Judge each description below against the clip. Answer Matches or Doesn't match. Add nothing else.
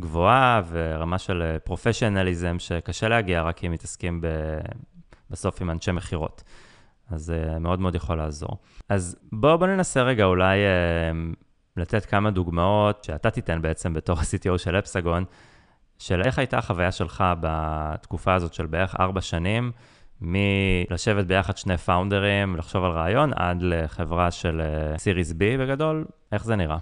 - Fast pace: Doesn't match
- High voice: Doesn't match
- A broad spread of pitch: Doesn't match